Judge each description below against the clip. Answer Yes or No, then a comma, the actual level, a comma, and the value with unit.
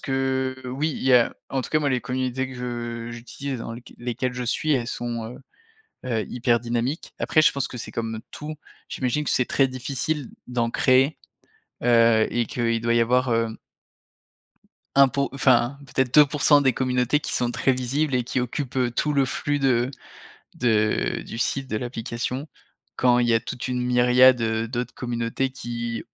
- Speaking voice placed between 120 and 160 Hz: Yes, low, 125 Hz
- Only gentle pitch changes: Yes, narrow, 2.1 semitones